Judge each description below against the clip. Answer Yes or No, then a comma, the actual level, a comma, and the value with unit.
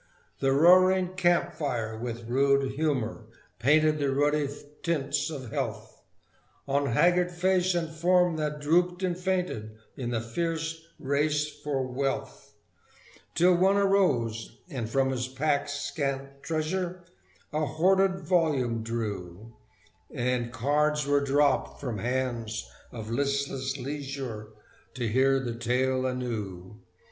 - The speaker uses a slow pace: Yes, slow, 120 wpm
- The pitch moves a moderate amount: Yes, average, 4.9 semitones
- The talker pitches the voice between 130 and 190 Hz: Yes, medium, 140 Hz